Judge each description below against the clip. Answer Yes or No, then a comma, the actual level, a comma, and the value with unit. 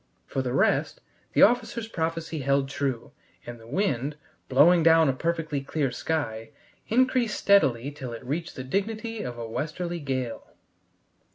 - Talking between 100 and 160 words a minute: Yes, average, 150 wpm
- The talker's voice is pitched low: No, medium, 150 Hz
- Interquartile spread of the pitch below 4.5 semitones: No, average, 5.2 semitones